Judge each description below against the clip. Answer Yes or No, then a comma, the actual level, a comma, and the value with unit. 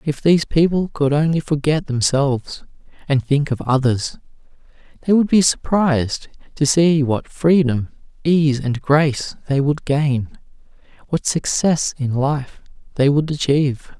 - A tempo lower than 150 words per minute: Yes, slow, 135 wpm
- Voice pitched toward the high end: No, medium, 145 Hz